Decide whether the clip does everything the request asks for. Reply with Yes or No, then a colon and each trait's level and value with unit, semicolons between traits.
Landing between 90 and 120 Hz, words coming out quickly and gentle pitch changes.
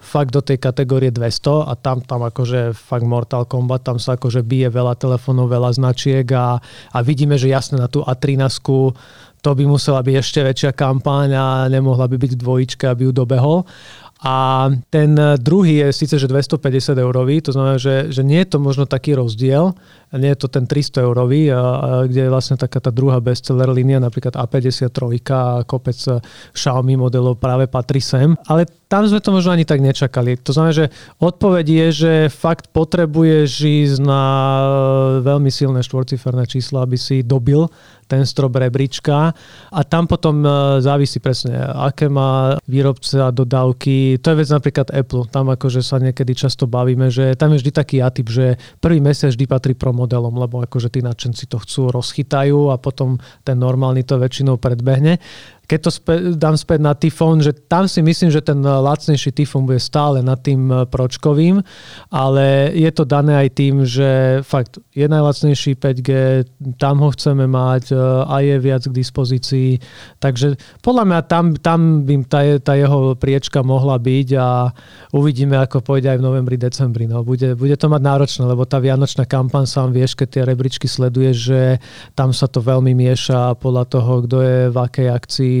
No: low, 135 Hz; fast, 175 wpm; narrow, 2.0 semitones